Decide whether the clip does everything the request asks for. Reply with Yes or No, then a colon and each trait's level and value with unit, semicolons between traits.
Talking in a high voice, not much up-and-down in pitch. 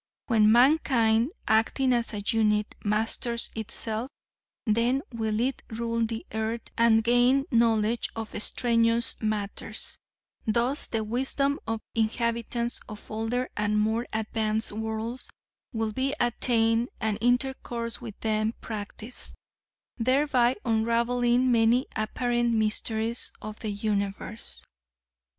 Yes: high, 230 Hz; narrow, 1.8 semitones